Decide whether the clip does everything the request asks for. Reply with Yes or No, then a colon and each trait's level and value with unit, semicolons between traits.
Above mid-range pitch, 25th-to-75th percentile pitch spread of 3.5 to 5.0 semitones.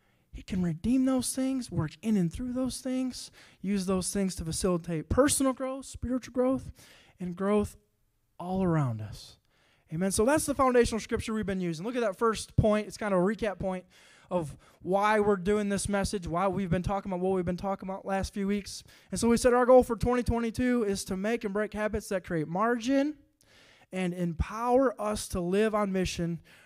Yes: high, 200 Hz; average, 4.6 semitones